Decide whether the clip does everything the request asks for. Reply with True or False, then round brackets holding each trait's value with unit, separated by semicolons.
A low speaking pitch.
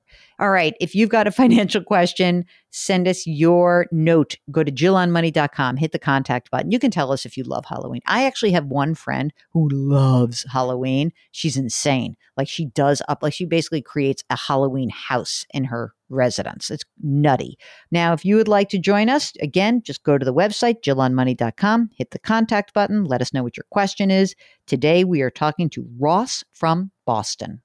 False (160 Hz)